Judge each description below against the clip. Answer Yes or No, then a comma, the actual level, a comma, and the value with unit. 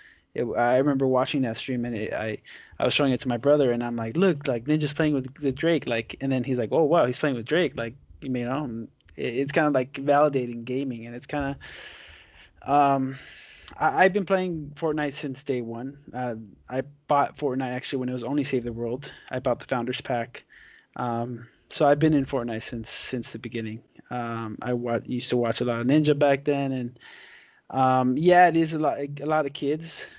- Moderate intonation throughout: Yes, average, 3.1 semitones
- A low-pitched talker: Yes, low, 130 Hz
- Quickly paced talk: Yes, fast, 220 wpm